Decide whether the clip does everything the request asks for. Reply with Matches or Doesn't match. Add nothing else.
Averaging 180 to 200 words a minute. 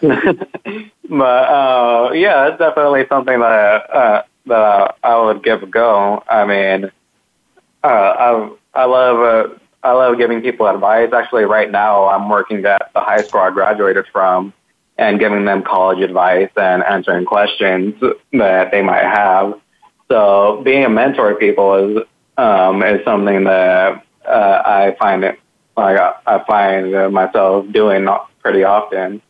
Doesn't match